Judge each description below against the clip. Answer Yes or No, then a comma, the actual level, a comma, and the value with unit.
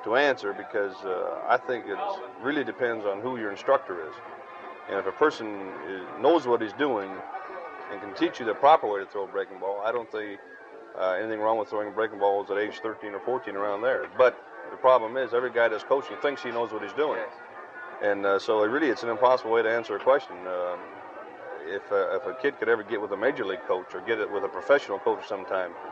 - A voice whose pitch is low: Yes, low, 125 Hz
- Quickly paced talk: Yes, fast, 230 wpm